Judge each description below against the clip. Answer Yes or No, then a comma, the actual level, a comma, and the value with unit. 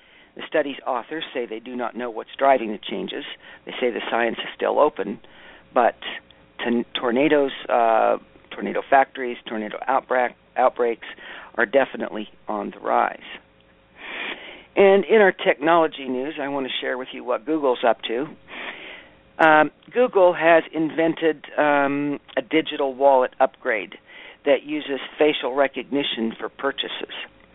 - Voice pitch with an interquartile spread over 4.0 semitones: Yes, average, 4.4 semitones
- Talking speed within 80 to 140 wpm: Yes, slow, 135 wpm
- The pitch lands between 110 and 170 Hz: Yes, medium, 140 Hz